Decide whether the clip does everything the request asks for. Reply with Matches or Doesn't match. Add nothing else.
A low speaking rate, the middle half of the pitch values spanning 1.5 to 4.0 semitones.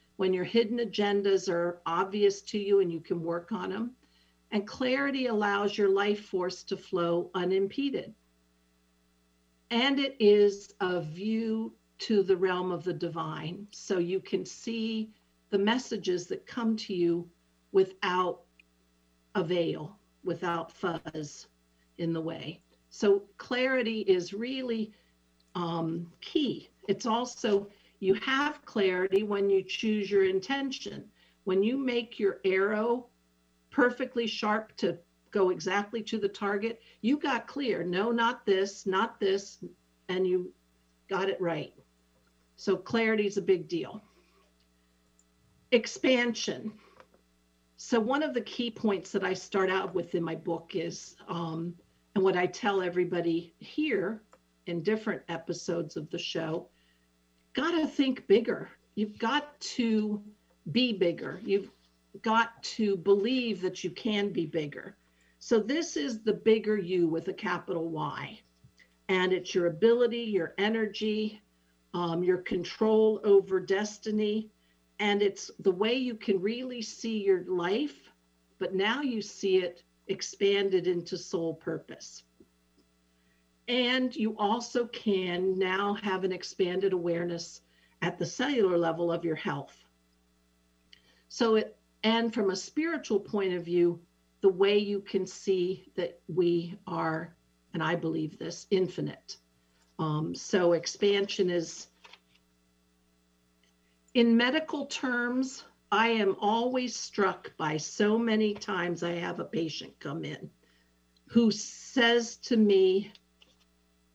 Doesn't match